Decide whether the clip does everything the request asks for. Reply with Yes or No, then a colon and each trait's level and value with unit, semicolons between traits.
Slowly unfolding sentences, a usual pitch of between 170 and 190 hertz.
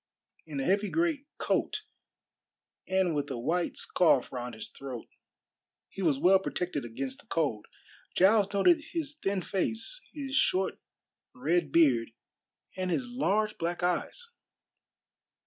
Yes: slow, 130 wpm; medium, 185 Hz